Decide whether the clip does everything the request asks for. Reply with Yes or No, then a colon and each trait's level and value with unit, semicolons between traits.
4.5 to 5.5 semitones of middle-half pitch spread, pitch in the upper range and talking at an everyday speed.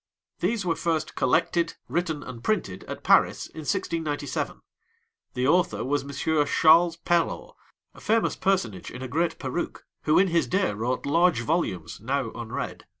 No: average, 5.1 semitones; medium, 155 Hz; average, 150 wpm